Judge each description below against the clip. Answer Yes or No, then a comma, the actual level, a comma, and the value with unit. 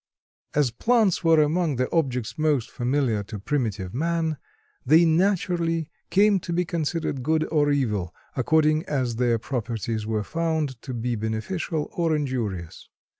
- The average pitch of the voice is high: No, medium, 145 Hz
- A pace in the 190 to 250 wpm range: No, average, 140 wpm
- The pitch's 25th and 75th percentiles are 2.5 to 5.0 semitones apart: No, wide, 5.6 semitones